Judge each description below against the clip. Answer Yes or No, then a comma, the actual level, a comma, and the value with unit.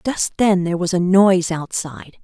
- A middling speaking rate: Yes, average, 190 wpm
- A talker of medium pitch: Yes, medium, 180 Hz